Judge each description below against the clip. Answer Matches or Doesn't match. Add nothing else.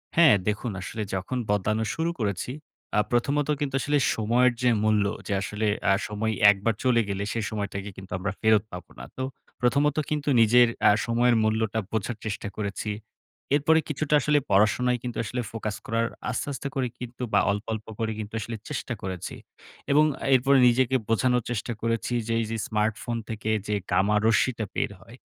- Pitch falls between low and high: Doesn't match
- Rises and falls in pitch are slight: Doesn't match